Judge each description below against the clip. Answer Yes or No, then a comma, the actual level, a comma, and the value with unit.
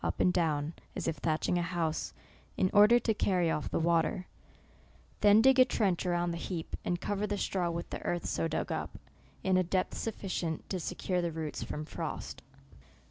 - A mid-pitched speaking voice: Yes, medium, 175 Hz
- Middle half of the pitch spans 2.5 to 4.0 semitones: Yes, average, 2.9 semitones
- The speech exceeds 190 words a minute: Yes, average, 200 wpm